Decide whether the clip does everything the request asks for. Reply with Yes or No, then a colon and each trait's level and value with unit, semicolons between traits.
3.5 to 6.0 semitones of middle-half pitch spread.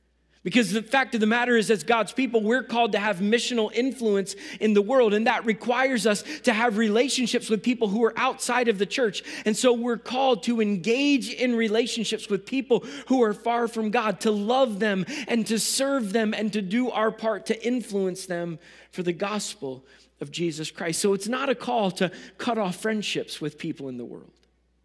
No: average, 3.1 semitones